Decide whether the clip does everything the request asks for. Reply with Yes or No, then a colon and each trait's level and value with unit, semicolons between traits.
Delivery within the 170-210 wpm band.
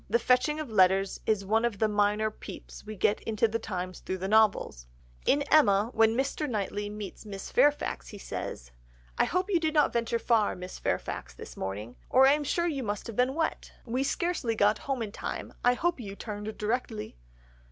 Yes: average, 200 wpm